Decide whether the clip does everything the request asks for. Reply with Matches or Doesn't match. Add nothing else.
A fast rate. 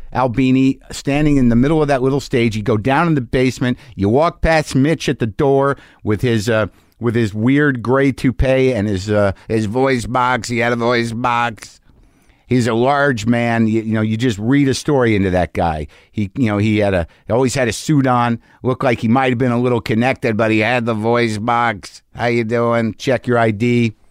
Matches